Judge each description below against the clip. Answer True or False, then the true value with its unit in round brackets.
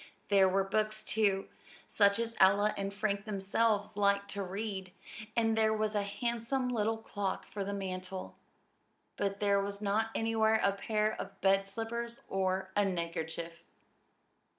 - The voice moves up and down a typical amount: False (2.0 semitones)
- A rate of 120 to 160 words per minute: True (150 wpm)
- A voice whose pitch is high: True (200 Hz)